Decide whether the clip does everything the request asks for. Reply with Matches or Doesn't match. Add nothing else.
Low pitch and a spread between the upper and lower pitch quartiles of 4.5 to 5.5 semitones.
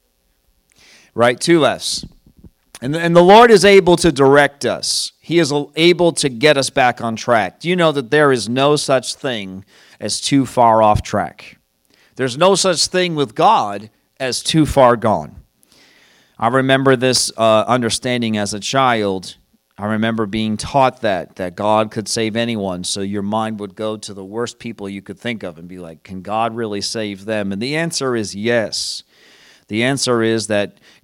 Matches